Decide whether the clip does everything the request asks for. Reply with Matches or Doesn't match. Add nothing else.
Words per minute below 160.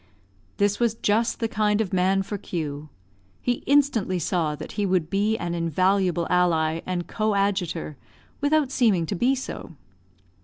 Matches